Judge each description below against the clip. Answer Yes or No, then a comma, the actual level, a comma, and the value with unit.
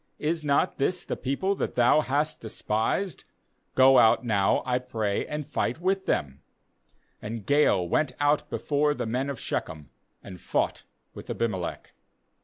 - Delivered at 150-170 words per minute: Yes, average, 155 wpm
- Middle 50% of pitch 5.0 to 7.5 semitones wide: Yes, average, 5.3 semitones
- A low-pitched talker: Yes, low, 130 Hz